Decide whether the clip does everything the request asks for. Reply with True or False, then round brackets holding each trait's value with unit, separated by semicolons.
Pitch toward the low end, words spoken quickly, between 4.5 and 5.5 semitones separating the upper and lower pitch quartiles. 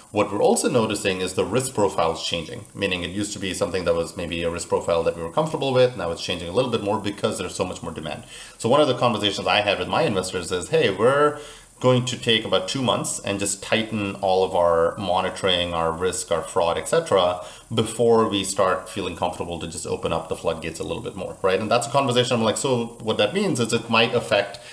True (110 Hz; 245 wpm; 4.8 semitones)